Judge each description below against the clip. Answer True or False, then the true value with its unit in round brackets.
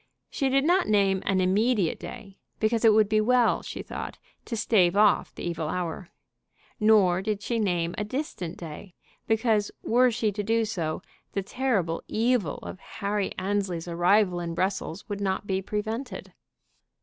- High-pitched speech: True (205 Hz)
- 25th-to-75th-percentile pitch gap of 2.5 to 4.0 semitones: True (3.4 semitones)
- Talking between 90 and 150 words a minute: False (160 wpm)